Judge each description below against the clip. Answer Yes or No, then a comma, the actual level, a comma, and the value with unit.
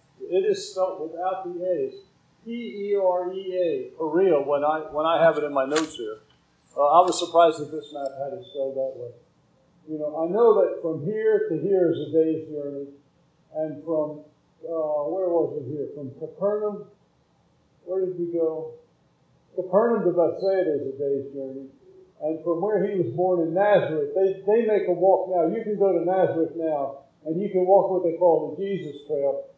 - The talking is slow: No, average, 190 wpm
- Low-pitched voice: No, medium, 170 Hz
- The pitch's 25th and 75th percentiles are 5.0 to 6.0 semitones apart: No, average, 4.3 semitones